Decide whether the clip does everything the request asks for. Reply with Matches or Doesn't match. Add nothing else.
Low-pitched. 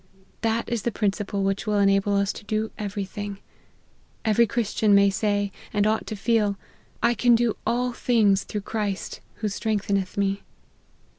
Doesn't match